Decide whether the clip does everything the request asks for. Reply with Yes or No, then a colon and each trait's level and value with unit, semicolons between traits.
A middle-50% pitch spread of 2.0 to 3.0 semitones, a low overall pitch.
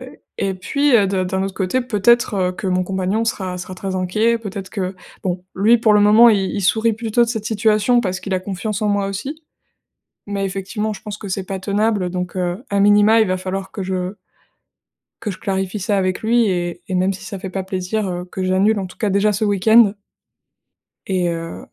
No: narrow, 2.6 semitones; high, 195 Hz